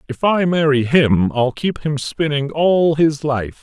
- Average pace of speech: Yes, average, 180 wpm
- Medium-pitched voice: Yes, medium, 145 Hz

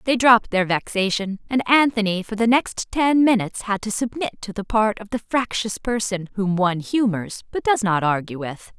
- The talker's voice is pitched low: No, high, 215 Hz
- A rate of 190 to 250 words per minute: Yes, average, 200 wpm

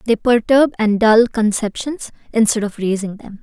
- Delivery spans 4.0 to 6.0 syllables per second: Yes, 4.6 syllables/s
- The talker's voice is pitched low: No, high, 225 Hz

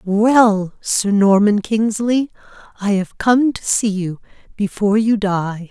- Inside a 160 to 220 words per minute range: No, slow, 135 wpm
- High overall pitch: Yes, high, 210 Hz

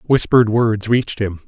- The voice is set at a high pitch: No, low, 110 Hz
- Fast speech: No, average, 165 wpm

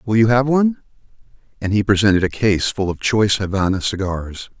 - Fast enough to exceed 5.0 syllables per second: Yes, 5.7 syllables/s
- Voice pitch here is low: Yes, low, 105 Hz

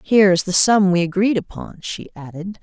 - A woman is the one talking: Yes, female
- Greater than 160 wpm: Yes, fast, 205 wpm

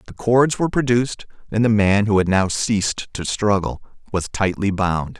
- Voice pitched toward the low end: Yes, low, 105 Hz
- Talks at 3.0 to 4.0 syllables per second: No, 4.9 syllables/s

